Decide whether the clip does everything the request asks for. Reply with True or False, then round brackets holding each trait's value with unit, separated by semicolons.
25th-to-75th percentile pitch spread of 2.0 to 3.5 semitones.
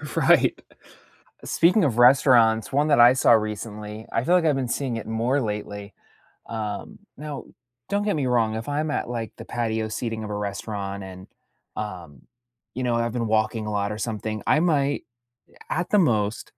False (4.1 semitones)